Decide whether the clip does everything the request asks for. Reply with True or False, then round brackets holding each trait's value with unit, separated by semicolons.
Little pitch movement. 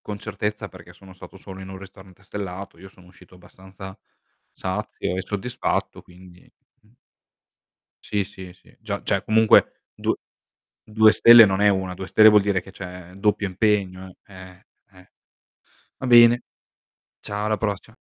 True (2.1 semitones)